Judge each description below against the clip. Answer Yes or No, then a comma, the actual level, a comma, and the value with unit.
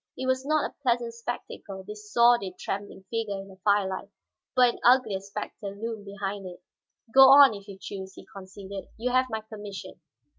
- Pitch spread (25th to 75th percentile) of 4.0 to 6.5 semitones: No, average, 3.4 semitones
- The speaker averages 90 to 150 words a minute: No, average, 180 wpm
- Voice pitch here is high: Yes, high, 210 Hz